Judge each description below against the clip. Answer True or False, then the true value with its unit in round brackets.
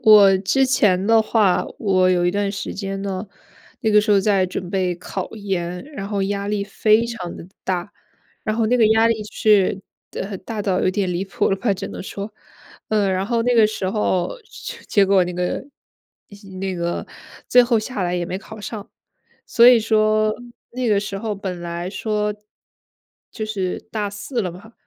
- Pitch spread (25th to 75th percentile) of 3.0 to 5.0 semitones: False (2.5 semitones)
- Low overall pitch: False (200 Hz)